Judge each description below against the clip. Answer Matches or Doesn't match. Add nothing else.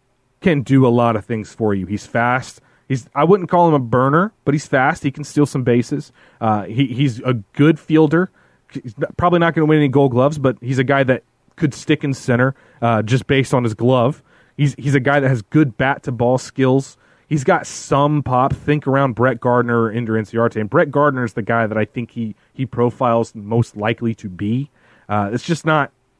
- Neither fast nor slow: Doesn't match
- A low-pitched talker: Matches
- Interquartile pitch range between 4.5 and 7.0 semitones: Doesn't match